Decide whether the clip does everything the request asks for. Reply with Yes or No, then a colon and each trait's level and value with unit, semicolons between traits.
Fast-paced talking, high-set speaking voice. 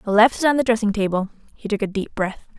Yes: fast, 255 wpm; high, 210 Hz